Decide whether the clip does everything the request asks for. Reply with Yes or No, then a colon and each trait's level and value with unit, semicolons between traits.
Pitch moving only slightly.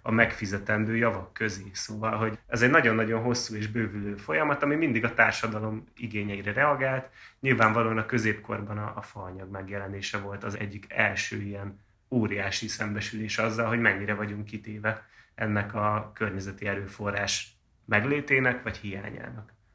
Yes: narrow, 1.8 semitones